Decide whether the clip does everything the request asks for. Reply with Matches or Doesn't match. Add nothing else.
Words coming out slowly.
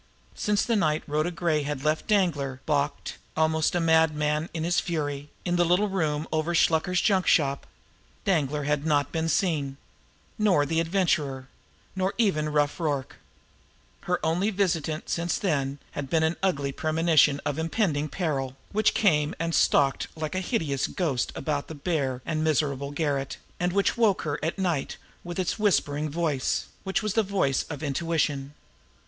Doesn't match